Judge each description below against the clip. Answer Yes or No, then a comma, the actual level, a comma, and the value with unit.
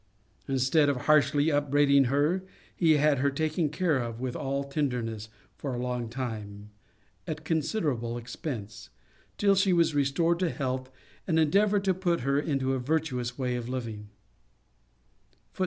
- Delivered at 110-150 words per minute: Yes, average, 145 wpm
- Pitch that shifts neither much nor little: Yes, average, 4.2 semitones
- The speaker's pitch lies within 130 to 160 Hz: Yes, medium, 140 Hz